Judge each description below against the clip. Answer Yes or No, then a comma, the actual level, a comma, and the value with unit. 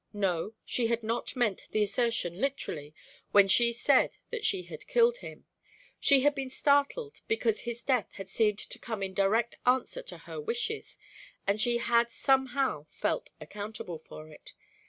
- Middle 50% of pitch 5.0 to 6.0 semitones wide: Yes, wide, 5.5 semitones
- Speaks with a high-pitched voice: Yes, high, 235 Hz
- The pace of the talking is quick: No, average, 165 wpm